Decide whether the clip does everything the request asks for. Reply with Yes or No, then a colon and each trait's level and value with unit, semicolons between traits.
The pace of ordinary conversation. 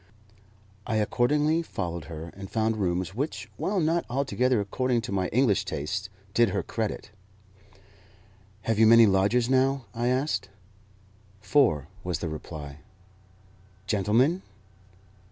No: slow, 120 wpm